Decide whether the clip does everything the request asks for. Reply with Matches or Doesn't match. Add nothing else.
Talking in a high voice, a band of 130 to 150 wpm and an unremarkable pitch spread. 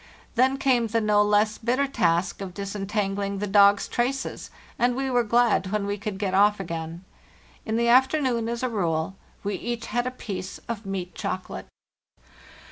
Doesn't match